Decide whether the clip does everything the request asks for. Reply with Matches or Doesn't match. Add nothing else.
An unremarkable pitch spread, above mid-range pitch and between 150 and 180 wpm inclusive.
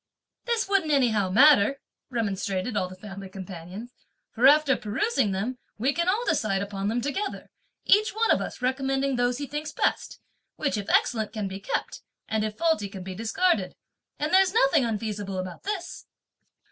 Doesn't match